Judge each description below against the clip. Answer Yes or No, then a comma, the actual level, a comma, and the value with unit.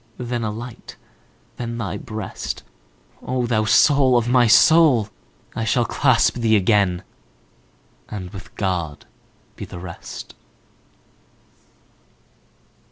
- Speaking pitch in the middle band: No, low, 115 Hz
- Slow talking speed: Yes, slow, 100 wpm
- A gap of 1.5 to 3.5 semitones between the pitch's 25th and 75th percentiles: No, average, 3.9 semitones